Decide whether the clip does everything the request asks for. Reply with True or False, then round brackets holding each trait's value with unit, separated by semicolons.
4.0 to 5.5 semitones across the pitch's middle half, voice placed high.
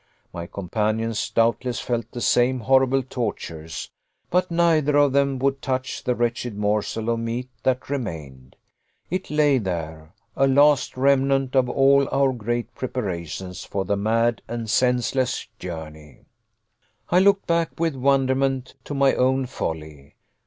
False (4.6 semitones; 125 Hz)